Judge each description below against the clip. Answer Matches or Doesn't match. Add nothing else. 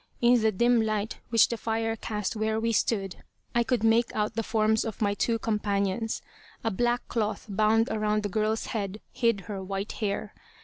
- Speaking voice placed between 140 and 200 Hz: Doesn't match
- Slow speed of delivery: Doesn't match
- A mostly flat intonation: Matches